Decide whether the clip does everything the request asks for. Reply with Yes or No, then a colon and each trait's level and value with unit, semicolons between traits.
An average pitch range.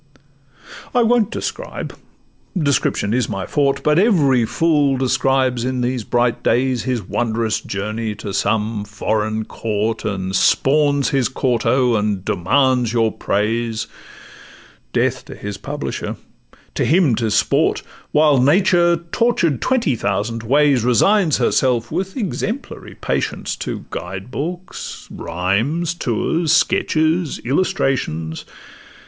No: wide, 5.8 semitones